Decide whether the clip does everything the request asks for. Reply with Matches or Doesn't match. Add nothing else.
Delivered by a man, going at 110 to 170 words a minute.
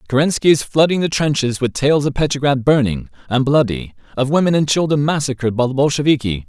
Doesn't match